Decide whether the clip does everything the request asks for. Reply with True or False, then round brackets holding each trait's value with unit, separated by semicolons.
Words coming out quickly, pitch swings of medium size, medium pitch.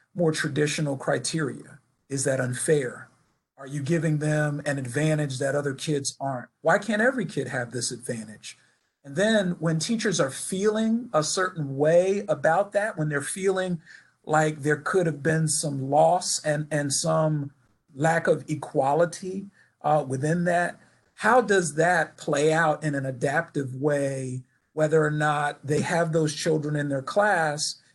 False (155 wpm; 3.2 semitones; 150 Hz)